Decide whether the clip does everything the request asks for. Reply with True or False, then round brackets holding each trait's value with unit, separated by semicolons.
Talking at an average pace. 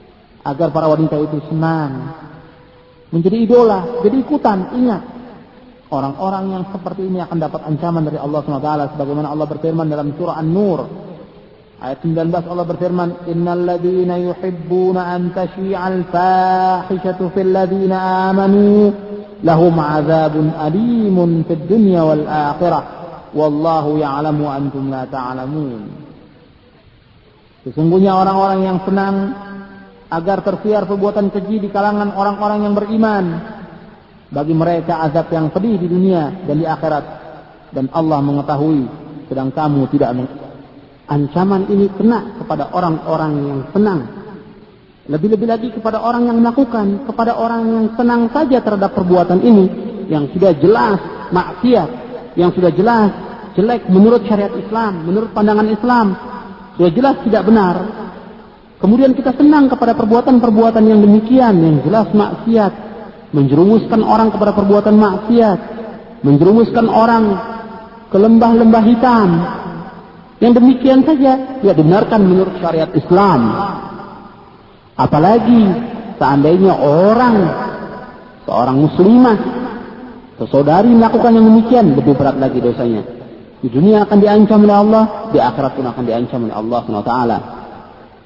False (120 wpm)